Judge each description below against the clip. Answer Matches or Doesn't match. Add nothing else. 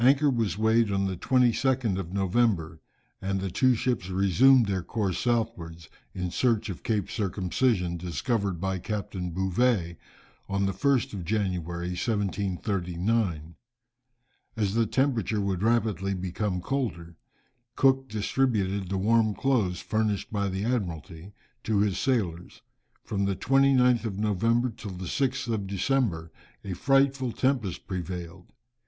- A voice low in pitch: Matches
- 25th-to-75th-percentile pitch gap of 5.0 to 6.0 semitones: Doesn't match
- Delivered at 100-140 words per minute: Matches